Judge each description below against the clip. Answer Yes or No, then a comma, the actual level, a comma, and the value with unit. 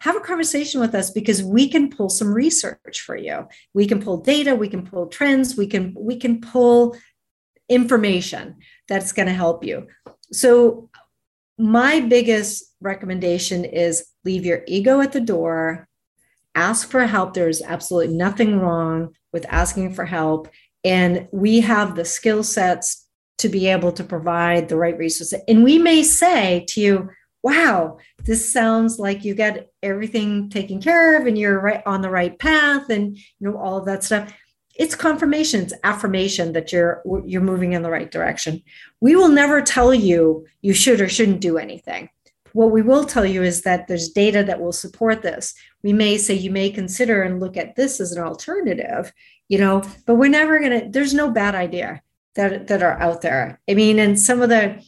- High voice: Yes, high, 200 Hz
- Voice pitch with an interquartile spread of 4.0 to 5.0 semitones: Yes, average, 4.7 semitones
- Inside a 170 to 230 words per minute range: Yes, average, 185 wpm